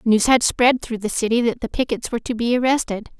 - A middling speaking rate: No, fast, 245 wpm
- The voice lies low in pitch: No, high, 235 Hz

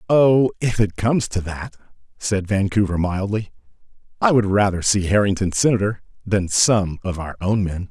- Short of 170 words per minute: Yes, average, 160 wpm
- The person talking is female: No, male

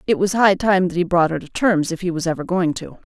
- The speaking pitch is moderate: Yes, medium, 175 Hz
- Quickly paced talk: Yes, fast, 310 wpm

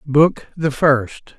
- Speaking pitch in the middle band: Yes, medium, 145 Hz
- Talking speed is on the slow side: Yes, slow, 130 wpm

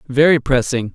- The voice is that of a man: Yes, male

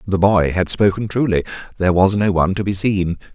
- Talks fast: Yes, fast, 215 wpm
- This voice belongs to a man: Yes, male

